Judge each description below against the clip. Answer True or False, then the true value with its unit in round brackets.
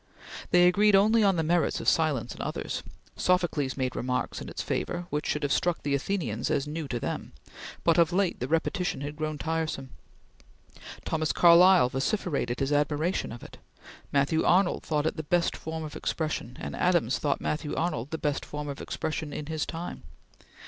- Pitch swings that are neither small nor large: True (3.4 semitones)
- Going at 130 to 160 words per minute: False (185 wpm)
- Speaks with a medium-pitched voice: True (155 Hz)